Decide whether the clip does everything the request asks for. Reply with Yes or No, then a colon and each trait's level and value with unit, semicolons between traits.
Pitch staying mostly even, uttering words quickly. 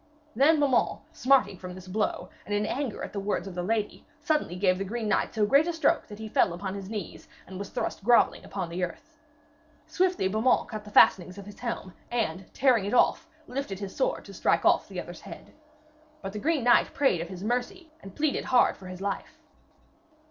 No: average, 5.3 semitones; fast, 215 wpm